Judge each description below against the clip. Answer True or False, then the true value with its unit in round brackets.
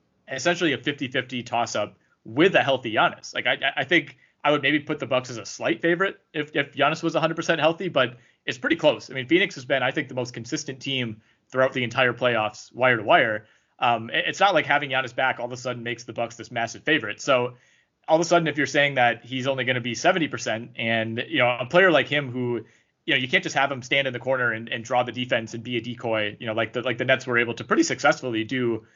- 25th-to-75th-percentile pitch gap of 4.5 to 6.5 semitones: False (3.5 semitones)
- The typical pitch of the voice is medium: False (130 Hz)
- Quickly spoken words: True (255 wpm)